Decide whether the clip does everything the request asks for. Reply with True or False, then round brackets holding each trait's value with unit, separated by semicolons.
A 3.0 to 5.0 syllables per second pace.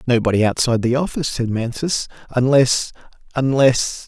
False (5.3 syllables/s)